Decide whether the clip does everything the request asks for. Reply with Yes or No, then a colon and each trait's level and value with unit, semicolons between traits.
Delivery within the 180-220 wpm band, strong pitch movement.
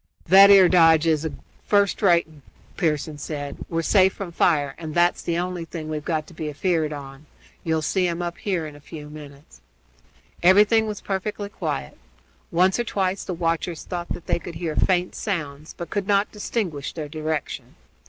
No: average, 185 wpm; average, 3.4 semitones